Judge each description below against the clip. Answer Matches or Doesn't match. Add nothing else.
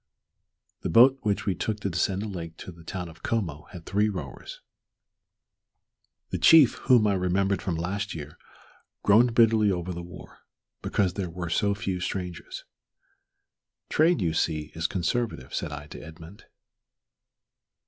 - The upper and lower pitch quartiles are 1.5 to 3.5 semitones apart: Doesn't match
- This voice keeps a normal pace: Matches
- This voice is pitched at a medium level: Doesn't match